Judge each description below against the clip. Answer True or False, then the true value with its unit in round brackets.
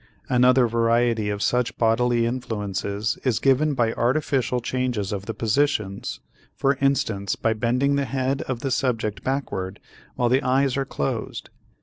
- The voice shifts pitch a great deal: False (3.3 semitones)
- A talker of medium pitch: False (120 Hz)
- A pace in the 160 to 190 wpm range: False (145 wpm)